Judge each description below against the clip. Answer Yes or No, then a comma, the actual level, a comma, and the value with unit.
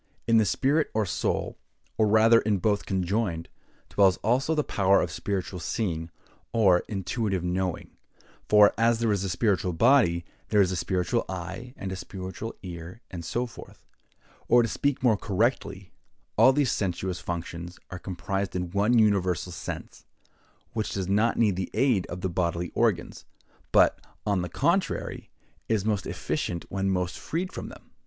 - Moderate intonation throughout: Yes, average, 3.9 semitones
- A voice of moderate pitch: No, low, 100 Hz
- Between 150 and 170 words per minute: Yes, average, 160 wpm